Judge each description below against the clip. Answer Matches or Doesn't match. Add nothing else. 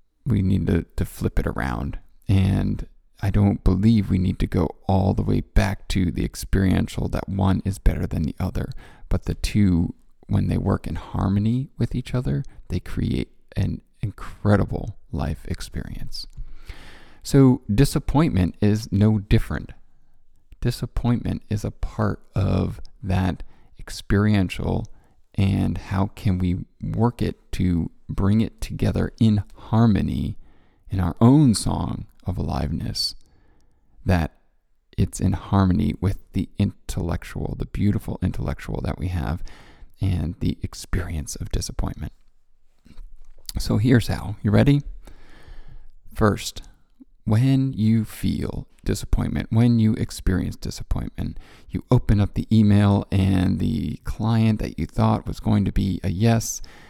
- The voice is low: Matches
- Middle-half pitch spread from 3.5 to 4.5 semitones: Matches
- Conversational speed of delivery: Doesn't match